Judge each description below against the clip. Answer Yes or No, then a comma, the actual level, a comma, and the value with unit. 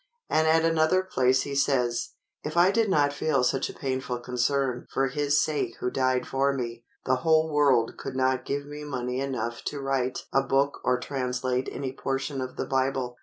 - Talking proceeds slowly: No, average, 190 wpm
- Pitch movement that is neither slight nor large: No, narrow, 2.2 semitones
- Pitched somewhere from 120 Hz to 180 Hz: Yes, low, 135 Hz